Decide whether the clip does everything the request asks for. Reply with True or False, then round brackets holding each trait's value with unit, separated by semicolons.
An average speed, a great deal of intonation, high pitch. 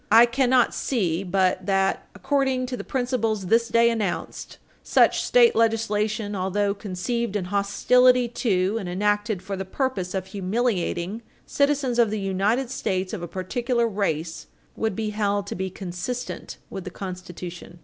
False (150 wpm; 4.0 semitones; 205 Hz)